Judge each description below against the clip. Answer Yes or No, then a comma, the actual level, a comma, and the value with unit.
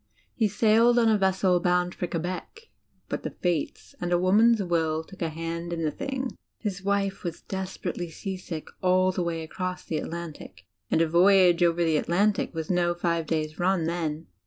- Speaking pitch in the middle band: Yes, medium, 175 Hz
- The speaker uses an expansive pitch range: No, narrow, 2.5 semitones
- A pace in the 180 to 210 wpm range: Yes, average, 185 wpm